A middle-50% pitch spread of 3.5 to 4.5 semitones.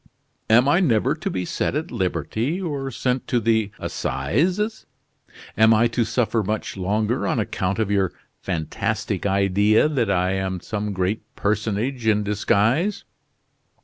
Yes: average, 4.0 semitones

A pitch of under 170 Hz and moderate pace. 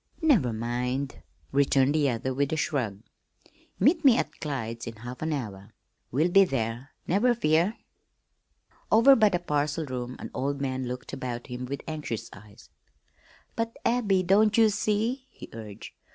Yes: medium, 140 Hz; average, 155 wpm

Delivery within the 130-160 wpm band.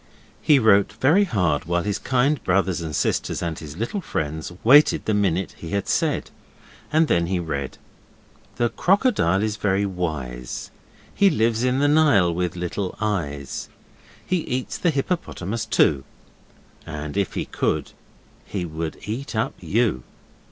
Yes: average, 150 wpm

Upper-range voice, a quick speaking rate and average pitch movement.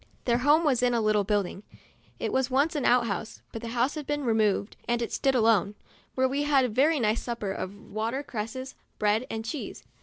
Yes: high, 235 Hz; fast, 220 wpm; average, 3.7 semitones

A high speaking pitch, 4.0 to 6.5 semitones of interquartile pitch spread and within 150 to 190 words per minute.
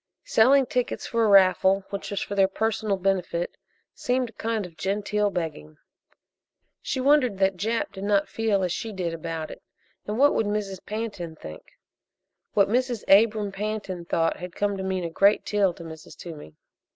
No: high, 200 Hz; average, 3.4 semitones; average, 175 wpm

